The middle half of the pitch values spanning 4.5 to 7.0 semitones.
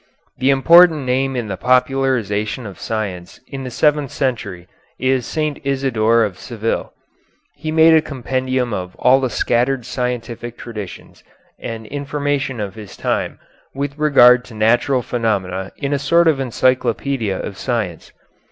No: average, 3.8 semitones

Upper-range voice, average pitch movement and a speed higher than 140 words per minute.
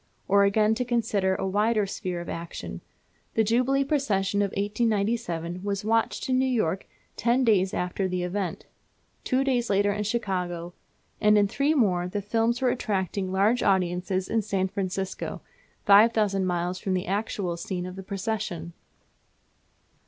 Yes: high, 200 Hz; average, 3.4 semitones; average, 150 wpm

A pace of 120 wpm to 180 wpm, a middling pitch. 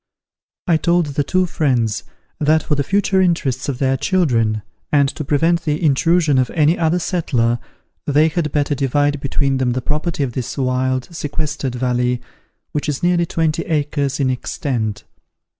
Yes: average, 160 wpm; medium, 145 Hz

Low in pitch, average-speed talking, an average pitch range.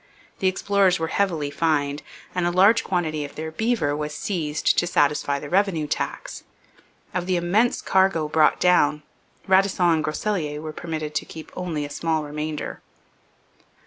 No: medium, 160 Hz; average, 155 wpm; average, 3.6 semitones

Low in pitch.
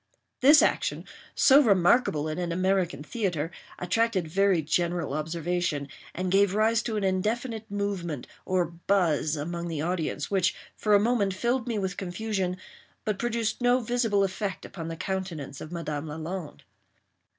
No: medium, 185 Hz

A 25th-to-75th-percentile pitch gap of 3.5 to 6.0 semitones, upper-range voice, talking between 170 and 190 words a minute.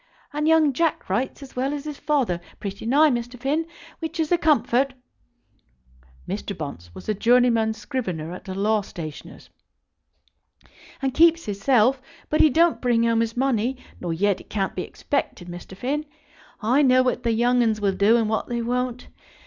Yes: average, 4.7 semitones; high, 245 Hz; average, 180 wpm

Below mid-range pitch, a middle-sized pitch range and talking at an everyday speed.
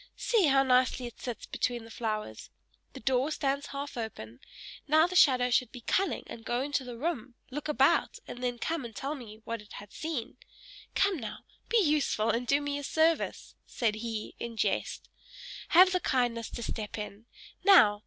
No: very high, 250 Hz; average, 4.4 semitones; average, 185 wpm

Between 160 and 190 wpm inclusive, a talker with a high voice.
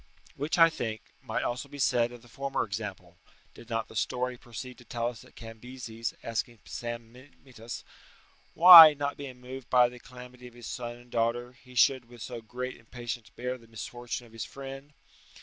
No: average, 185 wpm; low, 120 Hz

